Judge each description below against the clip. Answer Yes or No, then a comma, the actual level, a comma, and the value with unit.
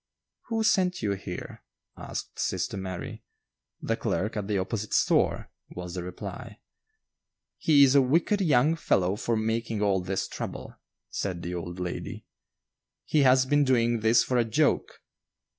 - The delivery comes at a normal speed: Yes, average, 150 wpm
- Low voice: Yes, low, 110 Hz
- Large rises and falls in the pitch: Yes, wide, 6.5 semitones